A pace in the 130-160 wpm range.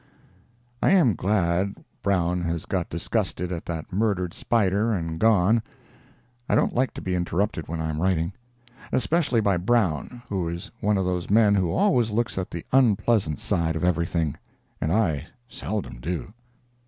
Yes: average, 155 wpm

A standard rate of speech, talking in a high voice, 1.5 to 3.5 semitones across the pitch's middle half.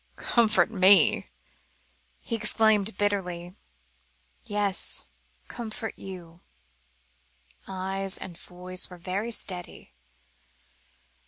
No: slow, 75 wpm; high, 195 Hz; average, 2.8 semitones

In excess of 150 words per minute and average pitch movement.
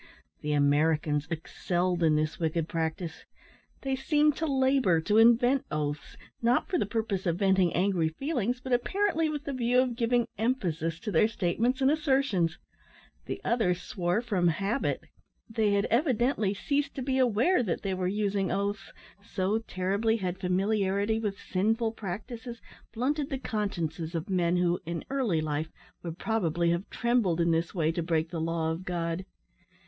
No: average, 165 wpm; wide, 6.0 semitones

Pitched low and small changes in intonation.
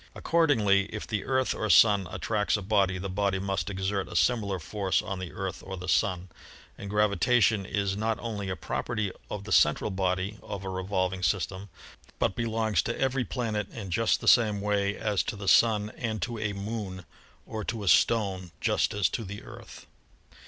Yes: low, 100 Hz; narrow, 2.3 semitones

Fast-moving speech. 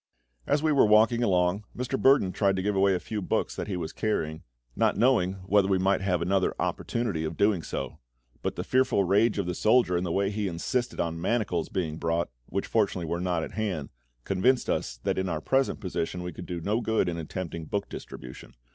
Yes: fast, 215 wpm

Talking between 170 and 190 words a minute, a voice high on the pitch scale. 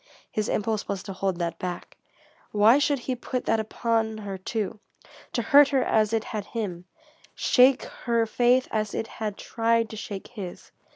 Yes: average, 175 wpm; high, 220 Hz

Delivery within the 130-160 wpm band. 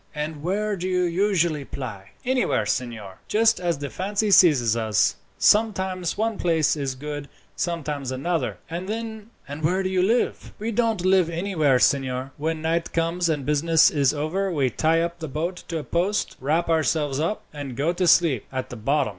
No: average, 175 wpm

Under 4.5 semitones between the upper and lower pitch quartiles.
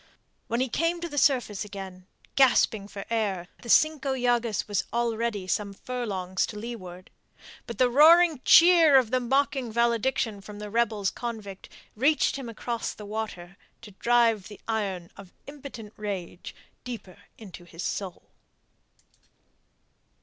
Yes: average, 4.1 semitones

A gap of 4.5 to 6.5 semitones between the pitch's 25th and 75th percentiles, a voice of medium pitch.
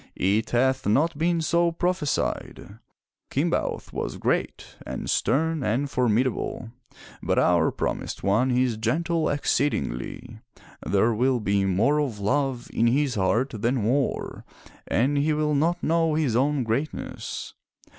No: average, 5.1 semitones; low, 130 Hz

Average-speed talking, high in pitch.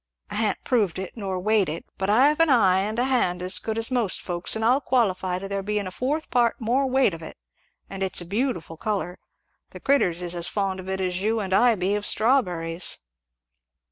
No: fast, 220 wpm; high, 200 Hz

